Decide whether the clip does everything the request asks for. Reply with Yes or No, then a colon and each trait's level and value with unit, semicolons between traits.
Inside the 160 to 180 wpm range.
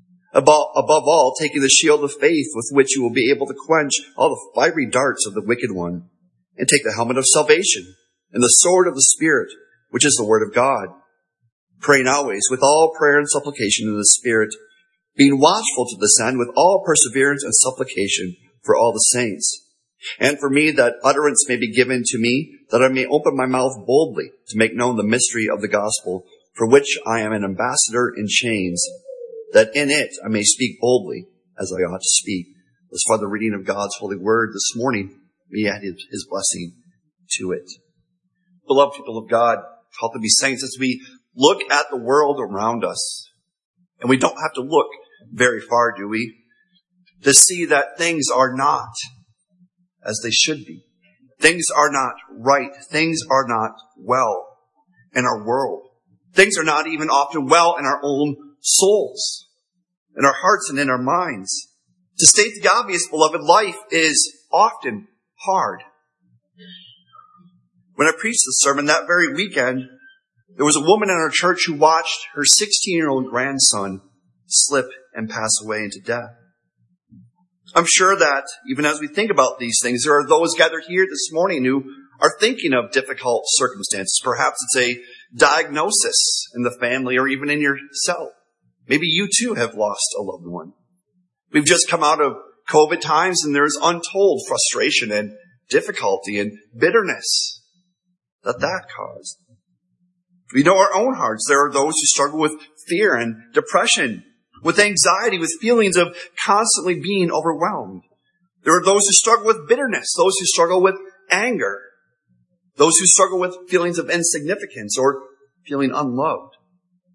Yes: average, 170 wpm